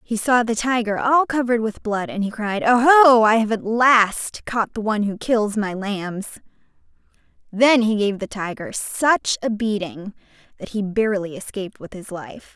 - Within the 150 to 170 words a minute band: No, average, 185 wpm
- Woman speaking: Yes, female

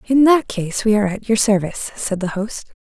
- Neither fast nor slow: No, fast, 235 wpm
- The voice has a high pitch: Yes, high, 215 Hz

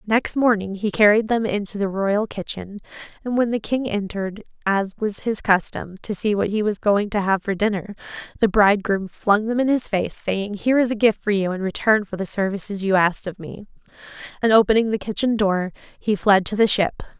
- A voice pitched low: No, high, 205 Hz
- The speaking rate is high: Yes, fast, 215 wpm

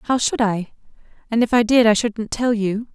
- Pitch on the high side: Yes, high, 225 Hz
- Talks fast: Yes, fast, 225 wpm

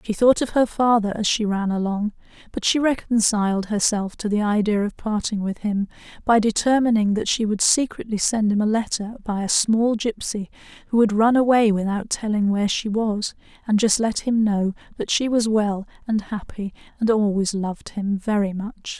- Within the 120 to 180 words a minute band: No, average, 190 wpm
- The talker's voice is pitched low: No, high, 215 Hz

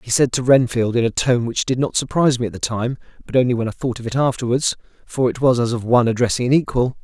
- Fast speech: Yes, fast, 265 wpm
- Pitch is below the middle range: Yes, low, 120 Hz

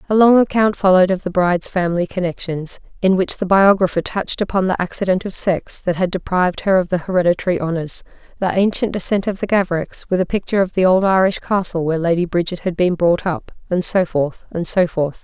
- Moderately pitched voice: Yes, medium, 180 Hz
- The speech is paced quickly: Yes, fast, 210 wpm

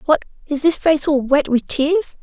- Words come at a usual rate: No, fast, 215 wpm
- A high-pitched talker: Yes, very high, 300 Hz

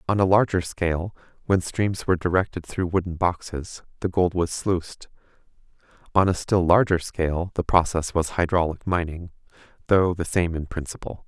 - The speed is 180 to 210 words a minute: No, average, 160 wpm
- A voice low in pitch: Yes, very low, 90 Hz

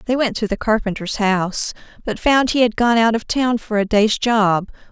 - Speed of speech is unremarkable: No, fast, 220 wpm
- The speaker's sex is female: Yes, female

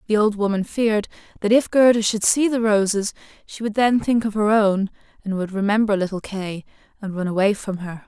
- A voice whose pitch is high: Yes, high, 210 Hz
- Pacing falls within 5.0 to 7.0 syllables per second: Yes, 5.3 syllables/s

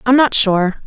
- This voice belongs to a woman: Yes, female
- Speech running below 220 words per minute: Yes, fast, 210 wpm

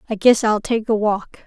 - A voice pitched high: Yes, high, 215 Hz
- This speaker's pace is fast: Yes, fast, 245 wpm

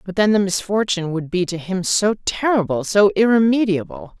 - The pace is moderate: Yes, average, 155 wpm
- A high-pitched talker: Yes, high, 195 Hz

